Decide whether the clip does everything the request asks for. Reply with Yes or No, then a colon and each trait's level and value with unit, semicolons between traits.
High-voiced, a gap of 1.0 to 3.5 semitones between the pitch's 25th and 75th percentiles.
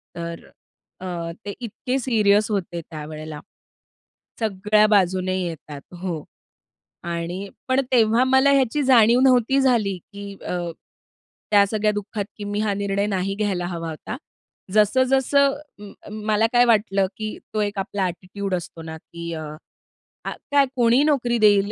No: high, 205 Hz; average, 4.1 semitones